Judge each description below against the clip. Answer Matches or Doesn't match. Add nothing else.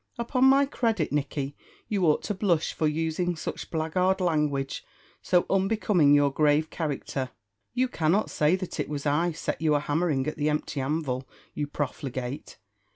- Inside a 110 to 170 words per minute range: Matches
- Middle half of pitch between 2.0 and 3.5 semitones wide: Doesn't match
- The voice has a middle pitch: Matches